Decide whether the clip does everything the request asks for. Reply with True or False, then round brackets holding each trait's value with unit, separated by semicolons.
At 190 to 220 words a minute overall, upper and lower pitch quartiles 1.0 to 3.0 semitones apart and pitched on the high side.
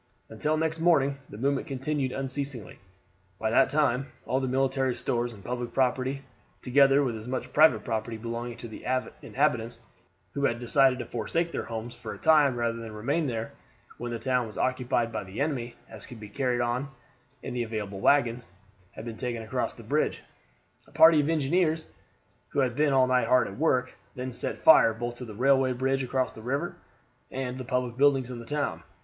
False (195 wpm; 2.7 semitones; 125 Hz)